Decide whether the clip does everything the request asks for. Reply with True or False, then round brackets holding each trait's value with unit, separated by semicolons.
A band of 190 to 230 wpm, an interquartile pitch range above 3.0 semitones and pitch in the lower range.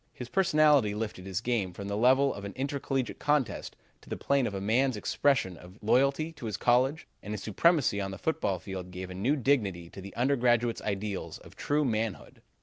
True (200 wpm; 5.6 semitones; 115 Hz)